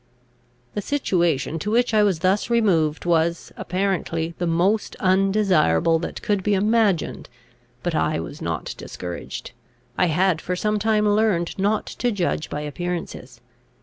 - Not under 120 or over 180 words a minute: Yes, average, 150 wpm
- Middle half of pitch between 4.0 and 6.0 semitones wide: Yes, average, 4.3 semitones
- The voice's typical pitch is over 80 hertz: Yes, medium, 185 Hz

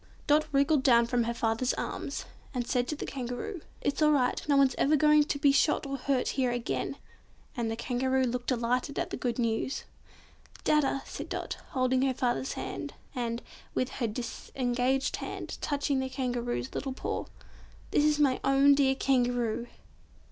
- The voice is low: No, very high, 260 Hz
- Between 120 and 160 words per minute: No, average, 170 wpm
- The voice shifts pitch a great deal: No, narrow, 2.4 semitones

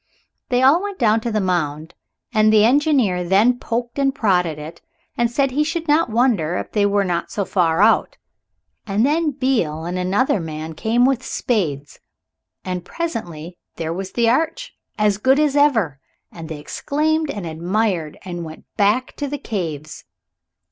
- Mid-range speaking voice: No, high, 215 Hz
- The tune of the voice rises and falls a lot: Yes, wide, 7.3 semitones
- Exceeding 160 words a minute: Yes, average, 170 wpm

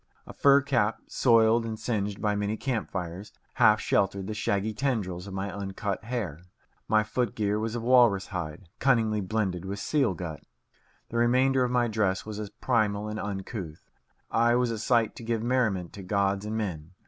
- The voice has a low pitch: Yes, low, 105 Hz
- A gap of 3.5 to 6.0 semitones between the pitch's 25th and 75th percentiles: No, average, 3.1 semitones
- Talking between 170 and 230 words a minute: Yes, average, 185 wpm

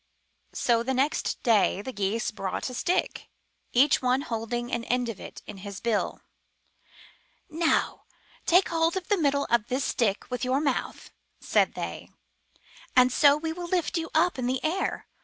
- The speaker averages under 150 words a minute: No, average, 170 wpm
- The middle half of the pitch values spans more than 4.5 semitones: Yes, average, 5.1 semitones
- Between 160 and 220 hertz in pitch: No, very high, 255 Hz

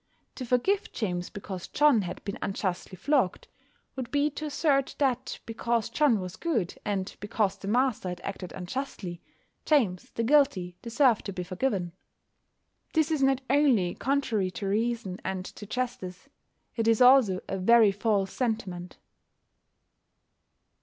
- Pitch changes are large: Yes, wide, 6.1 semitones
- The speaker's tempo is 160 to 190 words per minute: No, average, 140 wpm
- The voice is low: No, high, 225 Hz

